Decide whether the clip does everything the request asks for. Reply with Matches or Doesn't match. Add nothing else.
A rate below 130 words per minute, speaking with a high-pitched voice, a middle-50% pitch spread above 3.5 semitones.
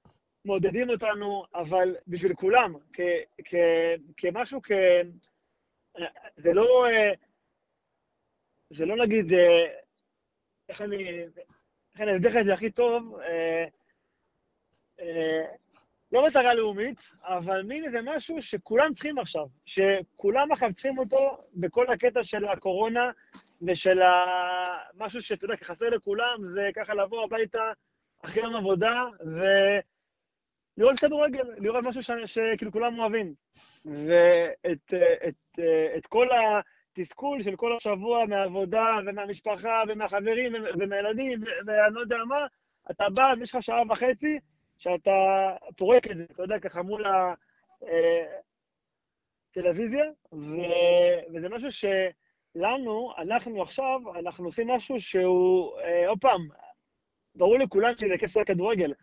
Matches